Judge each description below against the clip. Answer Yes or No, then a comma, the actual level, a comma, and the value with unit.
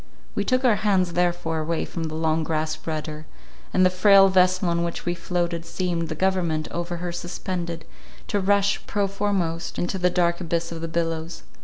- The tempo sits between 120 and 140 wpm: No, average, 185 wpm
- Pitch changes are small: Yes, narrow, 2.1 semitones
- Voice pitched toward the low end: No, medium, 175 Hz